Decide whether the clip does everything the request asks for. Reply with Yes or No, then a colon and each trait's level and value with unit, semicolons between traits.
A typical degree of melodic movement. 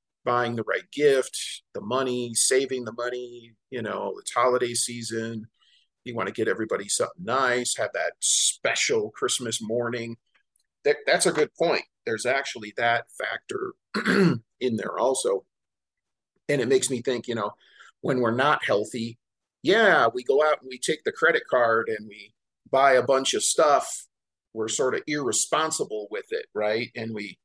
No: wide, 6.9 semitones